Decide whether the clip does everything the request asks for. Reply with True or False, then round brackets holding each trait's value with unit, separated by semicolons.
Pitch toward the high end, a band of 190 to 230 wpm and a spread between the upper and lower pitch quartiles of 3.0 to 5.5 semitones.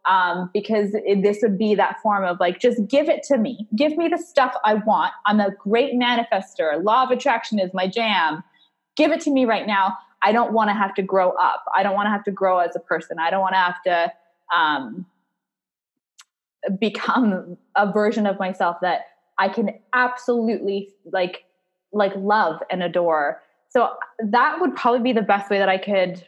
True (205 Hz; 200 wpm; 3.7 semitones)